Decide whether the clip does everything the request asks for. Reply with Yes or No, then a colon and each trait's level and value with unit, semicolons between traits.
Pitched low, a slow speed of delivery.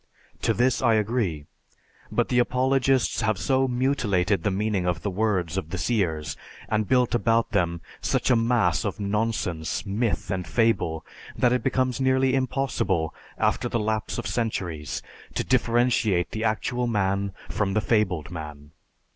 No: low, 110 Hz; average, 155 wpm